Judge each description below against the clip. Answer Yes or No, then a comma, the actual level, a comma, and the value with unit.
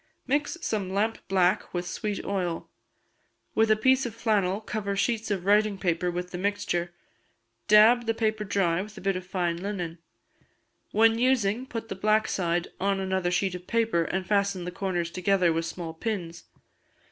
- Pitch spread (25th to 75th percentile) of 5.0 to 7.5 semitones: No, average, 3.4 semitones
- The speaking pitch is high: Yes, high, 195 Hz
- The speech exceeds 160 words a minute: Yes, average, 170 wpm